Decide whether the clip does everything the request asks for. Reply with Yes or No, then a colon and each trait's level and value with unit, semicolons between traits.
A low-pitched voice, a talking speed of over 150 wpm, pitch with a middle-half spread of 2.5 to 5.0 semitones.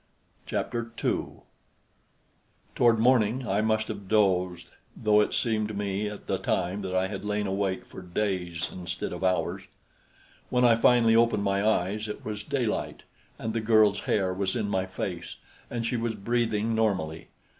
Yes: low, 105 Hz; average, 165 wpm; average, 3.1 semitones